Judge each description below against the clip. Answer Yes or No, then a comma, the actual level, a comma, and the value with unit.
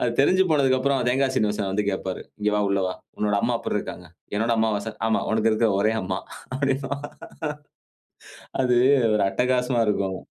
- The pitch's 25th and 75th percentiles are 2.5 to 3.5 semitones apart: No, average, 4.1 semitones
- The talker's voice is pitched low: Yes, low, 110 Hz